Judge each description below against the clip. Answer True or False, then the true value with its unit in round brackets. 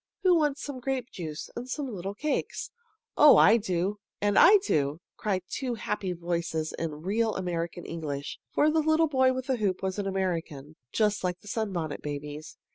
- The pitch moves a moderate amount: False (7.3 semitones)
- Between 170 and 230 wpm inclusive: True (180 wpm)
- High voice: True (195 Hz)